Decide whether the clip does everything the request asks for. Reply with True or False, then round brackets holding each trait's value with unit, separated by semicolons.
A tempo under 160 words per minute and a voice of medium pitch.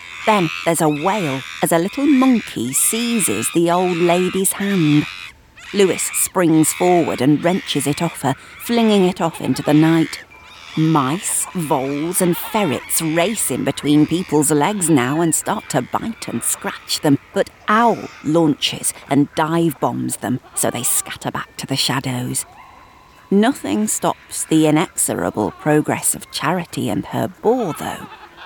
True (145 wpm; 160 Hz)